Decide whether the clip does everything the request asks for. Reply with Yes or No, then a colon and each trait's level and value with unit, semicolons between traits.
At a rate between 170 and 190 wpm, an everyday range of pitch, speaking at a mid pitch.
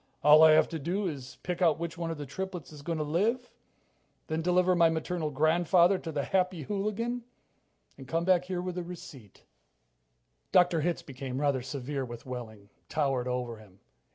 Yes: average, 180 wpm; average, 4.6 semitones; medium, 160 Hz